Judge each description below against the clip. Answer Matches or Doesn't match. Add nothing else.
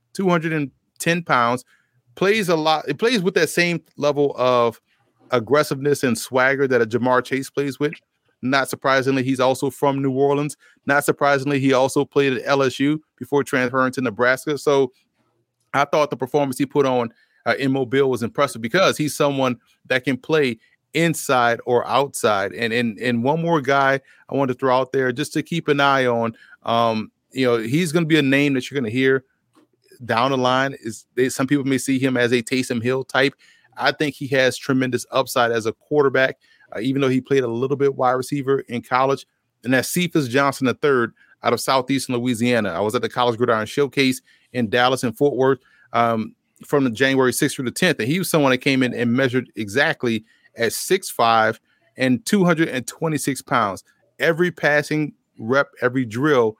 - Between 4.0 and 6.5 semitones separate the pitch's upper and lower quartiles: Doesn't match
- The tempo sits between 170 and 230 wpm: Matches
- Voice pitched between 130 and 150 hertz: Matches